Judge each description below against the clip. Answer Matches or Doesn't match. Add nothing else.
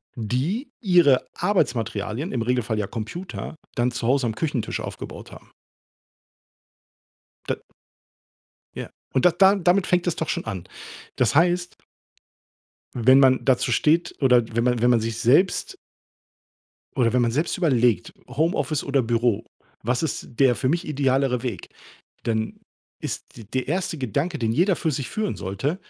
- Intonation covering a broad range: Matches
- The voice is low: Matches